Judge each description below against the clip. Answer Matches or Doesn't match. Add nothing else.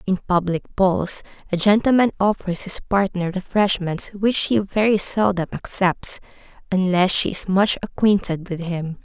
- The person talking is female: Matches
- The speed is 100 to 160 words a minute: Matches